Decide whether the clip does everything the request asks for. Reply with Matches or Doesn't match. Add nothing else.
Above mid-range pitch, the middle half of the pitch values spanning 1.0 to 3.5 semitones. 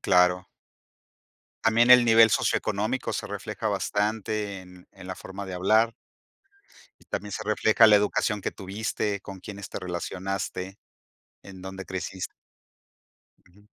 Doesn't match